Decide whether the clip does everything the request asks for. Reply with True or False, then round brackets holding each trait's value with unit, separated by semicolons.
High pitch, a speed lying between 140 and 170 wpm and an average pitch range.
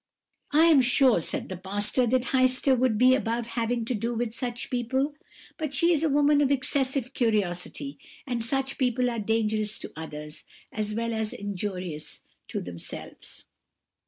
True (240 Hz; 160 wpm; 3.7 semitones)